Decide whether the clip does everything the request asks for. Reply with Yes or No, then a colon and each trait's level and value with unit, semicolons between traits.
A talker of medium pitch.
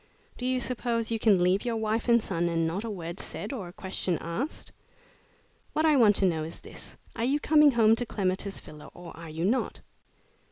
No: high, 210 Hz